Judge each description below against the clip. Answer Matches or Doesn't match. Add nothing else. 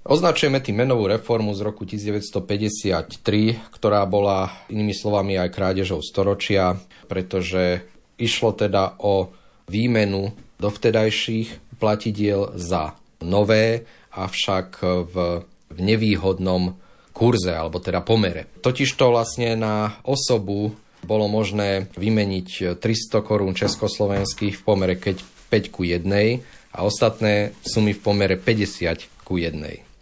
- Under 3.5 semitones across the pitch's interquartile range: Matches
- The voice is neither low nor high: Doesn't match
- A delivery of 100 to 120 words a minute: Matches